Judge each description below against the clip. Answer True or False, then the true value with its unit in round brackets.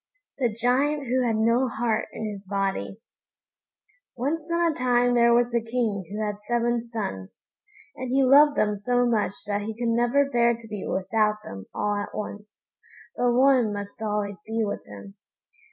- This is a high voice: True (230 Hz)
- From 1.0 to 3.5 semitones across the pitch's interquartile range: True (2.9 semitones)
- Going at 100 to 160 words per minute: False (175 wpm)